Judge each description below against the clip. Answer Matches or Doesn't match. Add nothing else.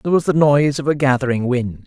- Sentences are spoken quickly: Matches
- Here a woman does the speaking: Doesn't match